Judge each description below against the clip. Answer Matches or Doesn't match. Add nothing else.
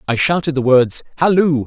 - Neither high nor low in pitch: Matches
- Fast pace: Doesn't match